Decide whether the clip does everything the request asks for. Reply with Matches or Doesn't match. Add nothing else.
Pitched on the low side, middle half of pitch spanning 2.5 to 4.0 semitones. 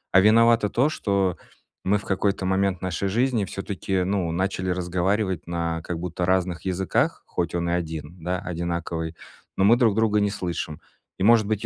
Matches